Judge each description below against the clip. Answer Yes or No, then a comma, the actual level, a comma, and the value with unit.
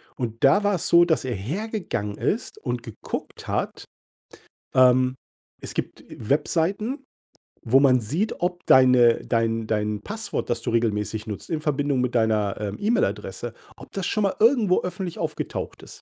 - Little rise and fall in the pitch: No, wide, 8.0 semitones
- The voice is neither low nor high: No, low, 130 Hz